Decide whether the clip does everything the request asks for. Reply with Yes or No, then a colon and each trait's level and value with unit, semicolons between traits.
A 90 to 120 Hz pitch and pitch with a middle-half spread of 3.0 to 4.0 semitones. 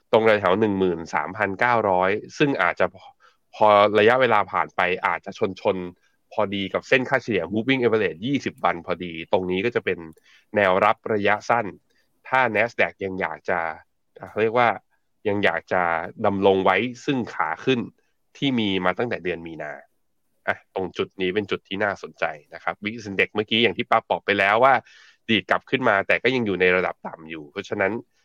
Yes: low, 100 Hz; average, 3.5 semitones